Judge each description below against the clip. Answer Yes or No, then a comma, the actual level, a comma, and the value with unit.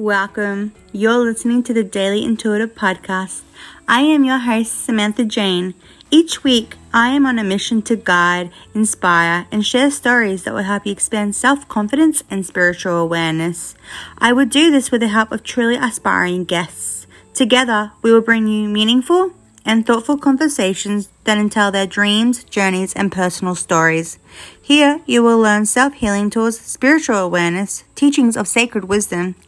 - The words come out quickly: No, average, 155 wpm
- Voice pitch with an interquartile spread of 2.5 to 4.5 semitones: Yes, average, 4.0 semitones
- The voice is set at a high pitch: Yes, high, 215 Hz